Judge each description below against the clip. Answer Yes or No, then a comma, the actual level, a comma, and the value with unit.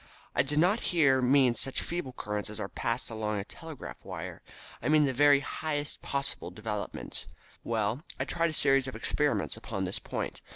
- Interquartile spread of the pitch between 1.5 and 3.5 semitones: No, average, 5.1 semitones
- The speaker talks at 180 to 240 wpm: Yes, average, 190 wpm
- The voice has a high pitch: No, low, 135 Hz